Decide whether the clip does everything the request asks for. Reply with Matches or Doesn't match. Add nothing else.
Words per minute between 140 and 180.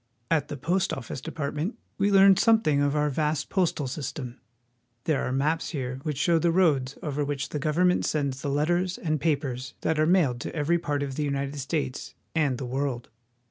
Doesn't match